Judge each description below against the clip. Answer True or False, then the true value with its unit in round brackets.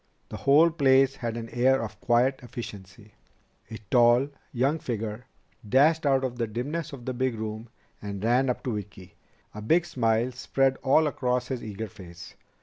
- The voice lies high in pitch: False (120 Hz)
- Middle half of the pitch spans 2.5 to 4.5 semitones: True (3.3 semitones)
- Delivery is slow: False (170 wpm)